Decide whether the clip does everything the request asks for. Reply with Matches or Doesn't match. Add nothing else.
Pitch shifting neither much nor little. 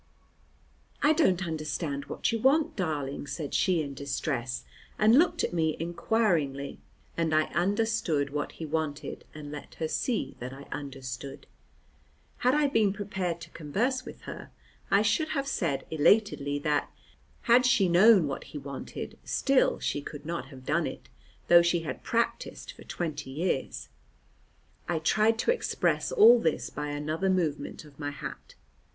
Doesn't match